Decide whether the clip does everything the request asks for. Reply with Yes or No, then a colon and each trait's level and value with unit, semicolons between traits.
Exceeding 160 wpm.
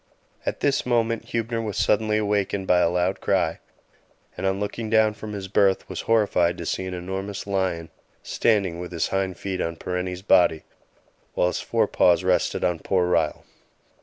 Yes: average, 170 wpm